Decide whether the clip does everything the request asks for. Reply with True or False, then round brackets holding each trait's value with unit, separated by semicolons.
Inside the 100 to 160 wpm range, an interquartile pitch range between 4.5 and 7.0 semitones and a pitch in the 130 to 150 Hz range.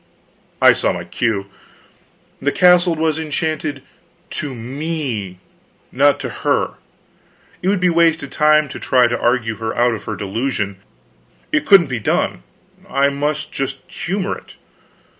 True (140 wpm; 5.4 semitones; 140 Hz)